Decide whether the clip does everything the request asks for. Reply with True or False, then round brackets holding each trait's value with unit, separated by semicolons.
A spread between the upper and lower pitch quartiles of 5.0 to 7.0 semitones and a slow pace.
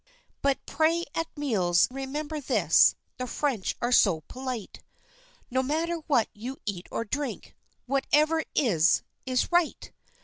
True (5.3 semitones; 130 wpm)